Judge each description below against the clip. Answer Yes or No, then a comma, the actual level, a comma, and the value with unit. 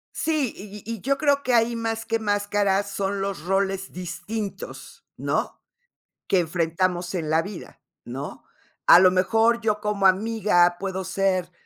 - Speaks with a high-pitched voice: Yes, high, 195 Hz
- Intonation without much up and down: No, average, 3.4 semitones